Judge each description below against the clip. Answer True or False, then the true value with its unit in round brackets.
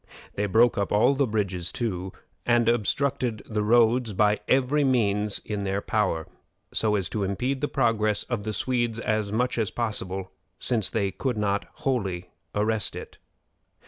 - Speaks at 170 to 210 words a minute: False (160 wpm)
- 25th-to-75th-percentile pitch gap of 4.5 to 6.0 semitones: False (3.0 semitones)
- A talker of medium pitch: False (110 Hz)